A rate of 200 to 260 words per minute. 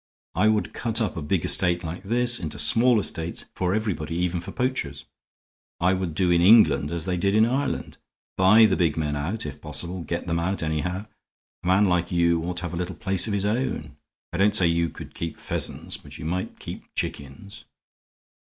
Yes: fast, 205 wpm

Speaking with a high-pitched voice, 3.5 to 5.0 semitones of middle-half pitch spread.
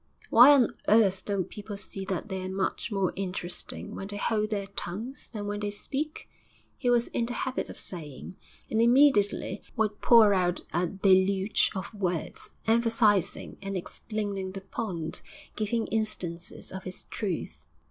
No: high, 200 Hz; average, 2.9 semitones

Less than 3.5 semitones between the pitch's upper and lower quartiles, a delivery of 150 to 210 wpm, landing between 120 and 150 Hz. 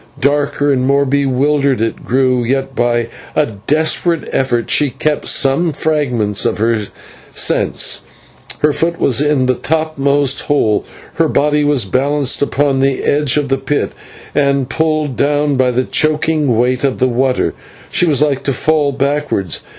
Yes: narrow, 2.5 semitones; average, 155 wpm; medium, 140 Hz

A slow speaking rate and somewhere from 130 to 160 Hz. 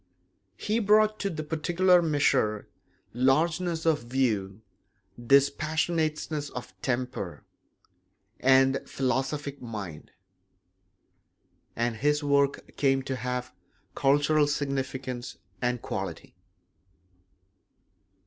Yes: slow, 85 wpm; medium, 140 Hz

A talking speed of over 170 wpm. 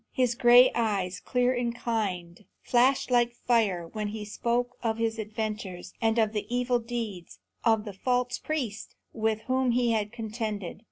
No: average, 160 wpm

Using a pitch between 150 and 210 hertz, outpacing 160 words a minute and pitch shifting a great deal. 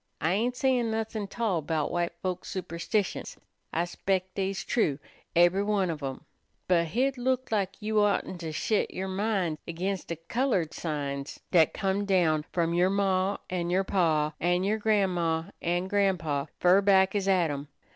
No: medium, 185 Hz; average, 170 wpm; average, 3.3 semitones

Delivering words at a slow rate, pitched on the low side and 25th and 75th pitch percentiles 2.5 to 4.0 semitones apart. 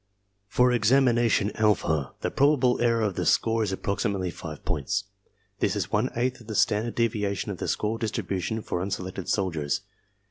No: average, 165 wpm; low, 105 Hz; average, 3.4 semitones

